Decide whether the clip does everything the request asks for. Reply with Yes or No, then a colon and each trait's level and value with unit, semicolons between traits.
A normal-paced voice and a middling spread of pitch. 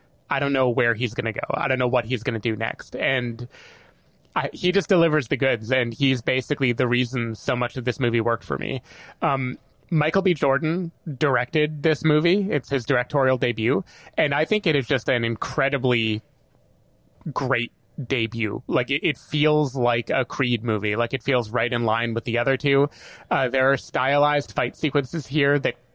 Yes: average, 195 wpm; average, 3.4 semitones